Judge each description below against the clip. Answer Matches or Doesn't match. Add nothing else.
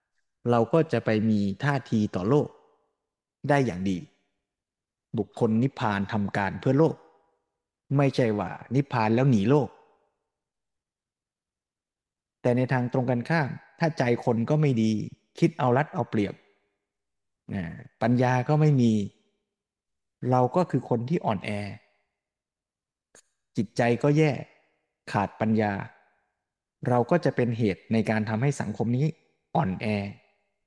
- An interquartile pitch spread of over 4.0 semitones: Matches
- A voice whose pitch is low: Matches